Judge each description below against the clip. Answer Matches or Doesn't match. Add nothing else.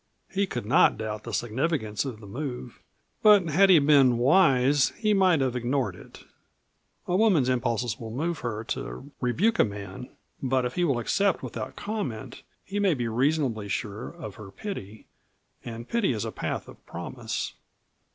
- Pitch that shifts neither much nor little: Doesn't match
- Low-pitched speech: Matches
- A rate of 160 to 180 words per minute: Matches